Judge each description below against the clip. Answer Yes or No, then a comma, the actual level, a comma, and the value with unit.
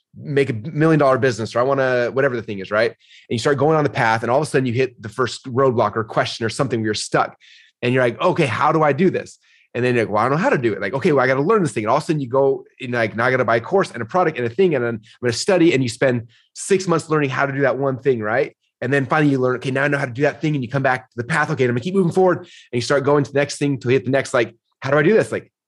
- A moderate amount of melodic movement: Yes, average, 3.4 semitones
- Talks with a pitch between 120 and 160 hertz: Yes, low, 135 Hz